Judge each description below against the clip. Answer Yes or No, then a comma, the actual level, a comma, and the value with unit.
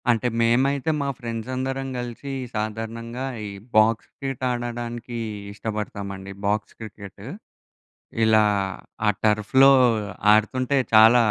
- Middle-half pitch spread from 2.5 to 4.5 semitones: Yes, average, 2.9 semitones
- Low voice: Yes, low, 115 Hz